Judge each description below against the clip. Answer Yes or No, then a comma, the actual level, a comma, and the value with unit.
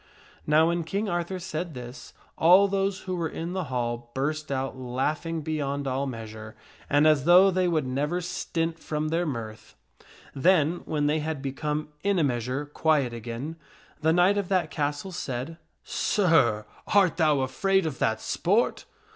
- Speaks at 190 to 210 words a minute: No, average, 165 wpm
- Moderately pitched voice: Yes, medium, 155 Hz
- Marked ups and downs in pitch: No, average, 4.7 semitones